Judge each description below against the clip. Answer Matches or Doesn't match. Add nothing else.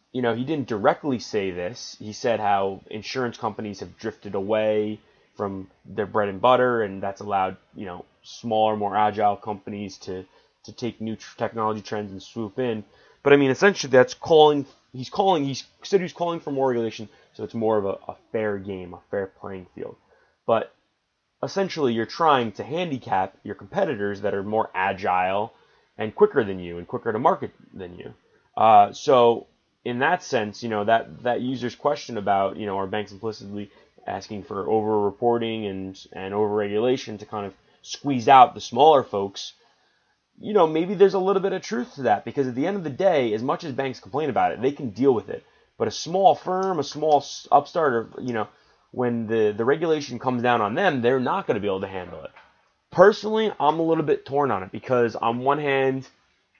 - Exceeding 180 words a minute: Matches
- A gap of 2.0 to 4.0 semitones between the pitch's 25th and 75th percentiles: Doesn't match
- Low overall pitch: Matches